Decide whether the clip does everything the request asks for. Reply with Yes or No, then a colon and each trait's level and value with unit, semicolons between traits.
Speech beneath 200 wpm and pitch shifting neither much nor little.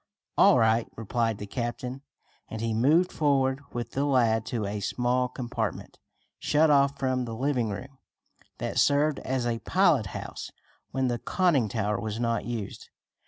Yes: average, 160 wpm; average, 3.5 semitones